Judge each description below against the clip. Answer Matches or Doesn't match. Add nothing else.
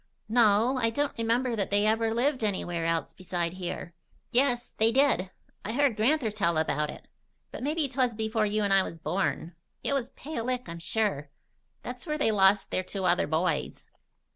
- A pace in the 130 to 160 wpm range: Doesn't match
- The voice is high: Matches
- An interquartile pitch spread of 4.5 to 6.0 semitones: Matches